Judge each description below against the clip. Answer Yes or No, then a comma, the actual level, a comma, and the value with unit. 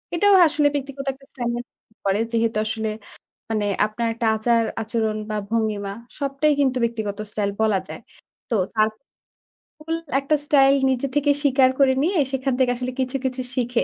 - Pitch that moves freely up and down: No, average, 3.8 semitones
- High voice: Yes, high, 245 Hz